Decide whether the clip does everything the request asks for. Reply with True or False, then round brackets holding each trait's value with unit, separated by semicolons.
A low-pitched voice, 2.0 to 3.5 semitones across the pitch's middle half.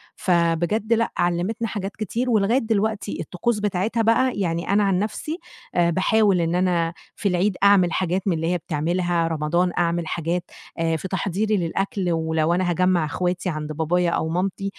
False (180 Hz; 3.2 semitones)